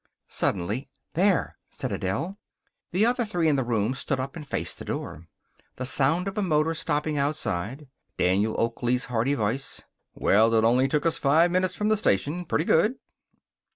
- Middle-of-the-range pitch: Yes, medium, 145 Hz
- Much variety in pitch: Yes, wide, 6.6 semitones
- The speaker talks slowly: No, average, 170 wpm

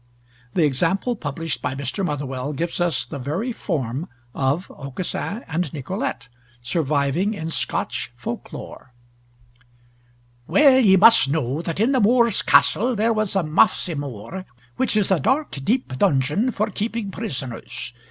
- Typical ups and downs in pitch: No, wide, 7.4 semitones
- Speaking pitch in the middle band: Yes, medium, 170 Hz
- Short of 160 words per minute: Yes, average, 140 wpm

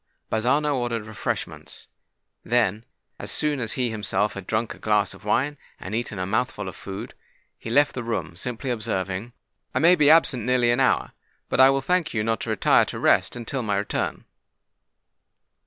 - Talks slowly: No, average, 180 wpm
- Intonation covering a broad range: No, average, 3.7 semitones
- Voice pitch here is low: Yes, low, 115 Hz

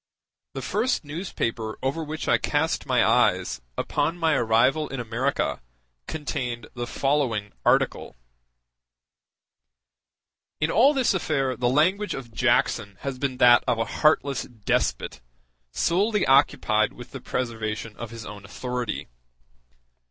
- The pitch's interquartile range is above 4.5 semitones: Yes, average, 4.9 semitones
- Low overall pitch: Yes, low, 125 Hz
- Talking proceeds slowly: Yes, slow, 125 wpm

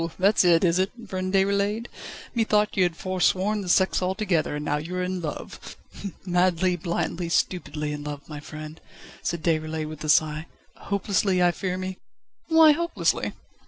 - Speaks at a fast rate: No, average, 160 wpm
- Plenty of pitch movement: No, average, 3.4 semitones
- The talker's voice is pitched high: No, medium, 180 Hz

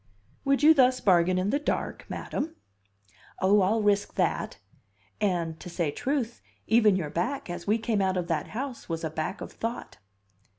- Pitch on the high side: Yes, high, 205 Hz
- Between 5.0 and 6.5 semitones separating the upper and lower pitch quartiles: Yes, wide, 5.6 semitones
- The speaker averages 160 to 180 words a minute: Yes, average, 175 wpm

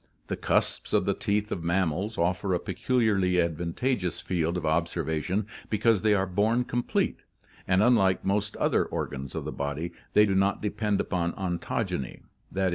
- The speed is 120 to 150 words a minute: No, average, 160 wpm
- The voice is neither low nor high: No, very low, 95 Hz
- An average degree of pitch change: Yes, average, 3.6 semitones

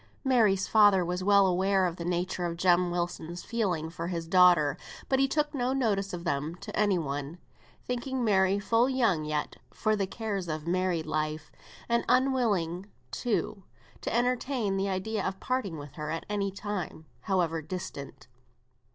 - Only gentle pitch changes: No, average, 4.3 semitones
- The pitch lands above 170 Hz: Yes, high, 190 Hz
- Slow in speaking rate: No, average, 165 wpm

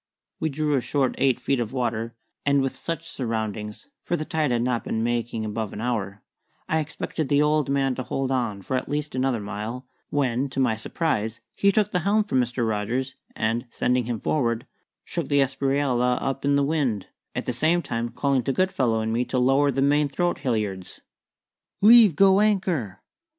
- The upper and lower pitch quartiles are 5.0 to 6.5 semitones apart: No, average, 4.0 semitones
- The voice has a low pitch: Yes, low, 130 Hz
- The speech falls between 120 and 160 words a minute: No, average, 190 wpm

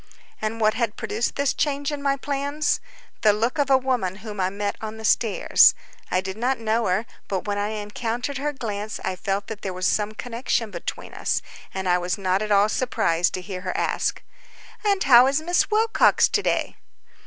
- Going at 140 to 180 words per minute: No, average, 200 wpm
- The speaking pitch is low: No, high, 220 Hz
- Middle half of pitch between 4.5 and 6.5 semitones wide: Yes, average, 4.9 semitones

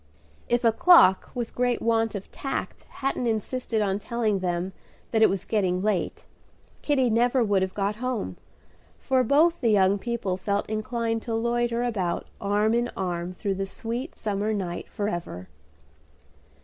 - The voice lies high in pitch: Yes, high, 220 Hz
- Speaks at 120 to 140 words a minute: No, average, 155 wpm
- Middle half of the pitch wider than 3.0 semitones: Yes, average, 3.7 semitones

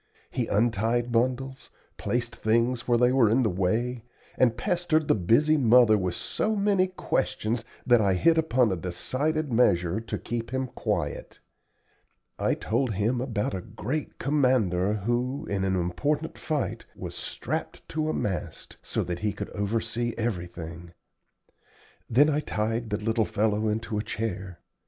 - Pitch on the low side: Yes, low, 115 Hz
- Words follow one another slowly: No, average, 150 wpm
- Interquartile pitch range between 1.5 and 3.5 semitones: No, average, 3.9 semitones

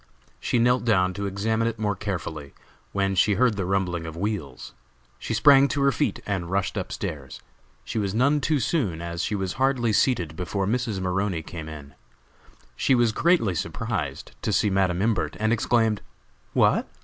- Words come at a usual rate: Yes, average, 175 wpm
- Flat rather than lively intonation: No, average, 4.5 semitones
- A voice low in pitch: Yes, low, 100 Hz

